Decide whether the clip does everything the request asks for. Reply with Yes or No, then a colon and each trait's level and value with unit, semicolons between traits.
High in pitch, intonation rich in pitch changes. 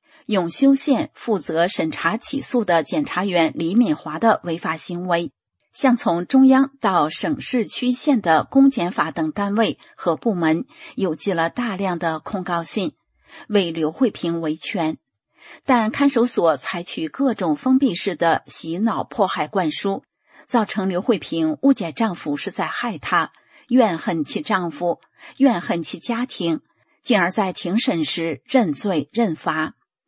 Yes: high, 210 Hz; wide, 7.5 semitones